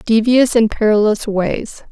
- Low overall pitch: No, high, 220 Hz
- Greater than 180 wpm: No, slow, 125 wpm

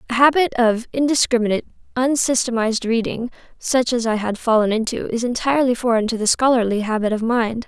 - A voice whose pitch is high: Yes, high, 235 Hz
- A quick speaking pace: No, average, 165 wpm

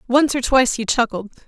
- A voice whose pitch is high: Yes, high, 245 Hz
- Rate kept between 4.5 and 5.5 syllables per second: No, 6.0 syllables/s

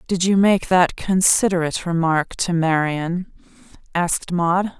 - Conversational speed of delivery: No, slow, 125 wpm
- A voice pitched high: No, medium, 175 Hz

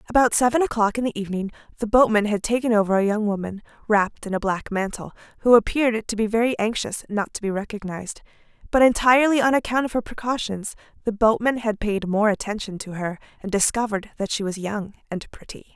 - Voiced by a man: No, female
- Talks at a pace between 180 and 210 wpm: Yes, average, 200 wpm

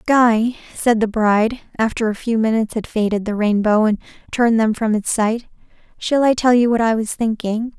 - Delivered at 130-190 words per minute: No, average, 200 wpm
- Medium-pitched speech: No, high, 225 Hz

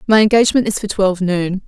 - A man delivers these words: No, female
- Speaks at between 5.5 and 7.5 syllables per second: Yes, 6.8 syllables/s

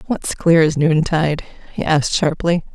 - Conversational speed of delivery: Yes, average, 155 wpm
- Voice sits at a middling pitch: Yes, medium, 160 Hz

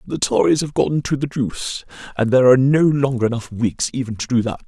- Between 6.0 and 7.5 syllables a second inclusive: Yes, 6.1 syllables/s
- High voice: No, low, 125 Hz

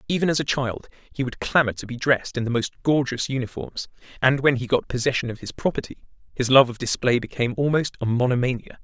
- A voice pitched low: Yes, low, 125 Hz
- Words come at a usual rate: No, fast, 210 wpm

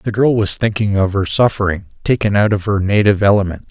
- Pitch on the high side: No, low, 100 Hz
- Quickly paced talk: Yes, fast, 210 wpm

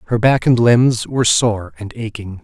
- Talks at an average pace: Yes, average, 195 wpm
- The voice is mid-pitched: No, low, 110 Hz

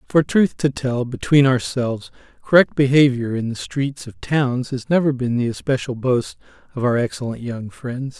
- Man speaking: Yes, male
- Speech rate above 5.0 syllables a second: No, 4.8 syllables/s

